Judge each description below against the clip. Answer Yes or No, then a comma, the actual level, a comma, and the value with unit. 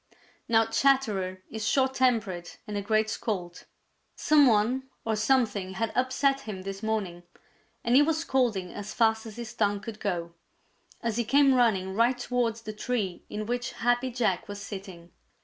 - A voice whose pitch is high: Yes, high, 220 Hz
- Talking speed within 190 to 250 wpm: No, average, 165 wpm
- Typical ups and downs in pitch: Yes, average, 3.7 semitones